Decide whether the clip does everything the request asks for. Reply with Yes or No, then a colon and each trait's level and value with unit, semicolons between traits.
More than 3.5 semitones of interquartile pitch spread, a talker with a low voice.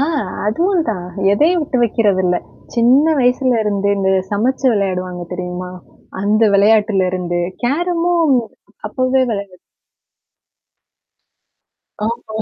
No: average, 5.3 semitones; high, 215 Hz